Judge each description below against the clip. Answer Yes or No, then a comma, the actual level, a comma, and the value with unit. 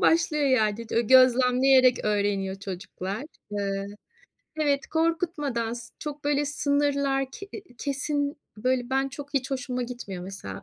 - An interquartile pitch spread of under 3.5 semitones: No, average, 4.1 semitones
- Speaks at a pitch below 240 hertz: No, very high, 260 Hz